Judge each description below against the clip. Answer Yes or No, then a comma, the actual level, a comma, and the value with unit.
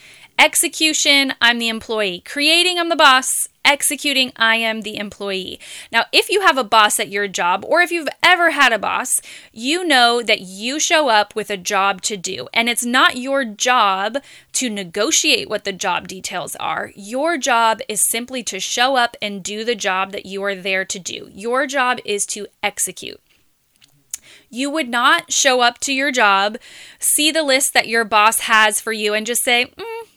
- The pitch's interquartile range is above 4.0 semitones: Yes, wide, 5.5 semitones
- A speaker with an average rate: Yes, average, 190 wpm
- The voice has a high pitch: Yes, high, 240 Hz